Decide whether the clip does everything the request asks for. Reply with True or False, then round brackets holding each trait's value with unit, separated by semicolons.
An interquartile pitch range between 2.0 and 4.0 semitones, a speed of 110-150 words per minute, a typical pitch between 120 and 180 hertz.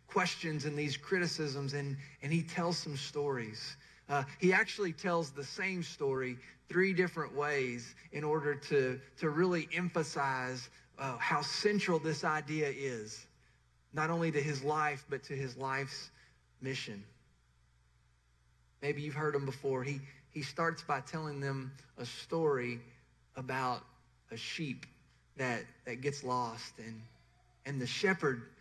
True (3.7 semitones; 140 wpm; 140 Hz)